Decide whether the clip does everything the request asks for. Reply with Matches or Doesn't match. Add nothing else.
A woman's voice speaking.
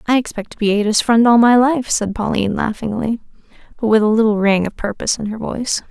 Matches